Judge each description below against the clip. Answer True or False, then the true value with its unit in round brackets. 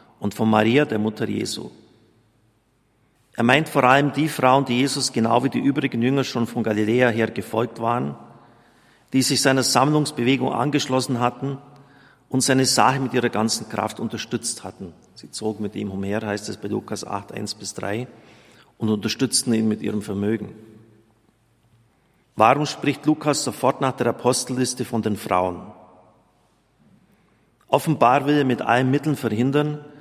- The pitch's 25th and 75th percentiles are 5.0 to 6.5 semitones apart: False (3.5 semitones)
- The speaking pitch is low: True (120 Hz)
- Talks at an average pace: True (150 wpm)